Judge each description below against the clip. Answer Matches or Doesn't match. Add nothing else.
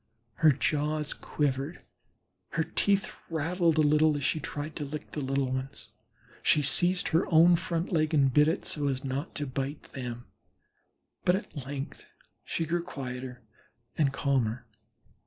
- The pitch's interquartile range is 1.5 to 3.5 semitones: Matches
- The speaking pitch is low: Doesn't match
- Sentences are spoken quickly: Doesn't match